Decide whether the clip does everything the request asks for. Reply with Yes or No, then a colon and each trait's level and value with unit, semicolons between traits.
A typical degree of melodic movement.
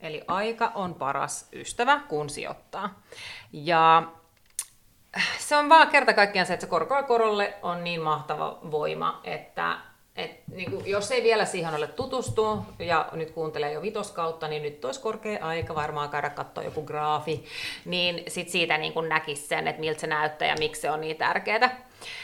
No: wide, 6.3 semitones